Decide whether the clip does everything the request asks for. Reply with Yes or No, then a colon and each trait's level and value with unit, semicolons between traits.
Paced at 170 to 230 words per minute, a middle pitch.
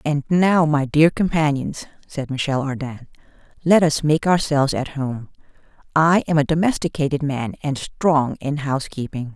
No: average, 145 wpm; medium, 150 Hz